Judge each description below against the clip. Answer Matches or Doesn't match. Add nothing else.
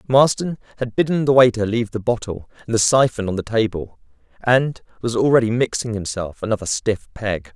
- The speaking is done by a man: Matches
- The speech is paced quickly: Doesn't match